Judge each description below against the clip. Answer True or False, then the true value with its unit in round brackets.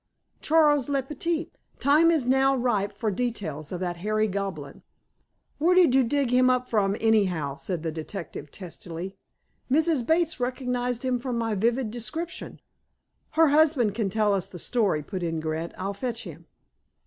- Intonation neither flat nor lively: False (6.1 semitones)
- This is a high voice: True (230 Hz)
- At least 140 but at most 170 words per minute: True (160 wpm)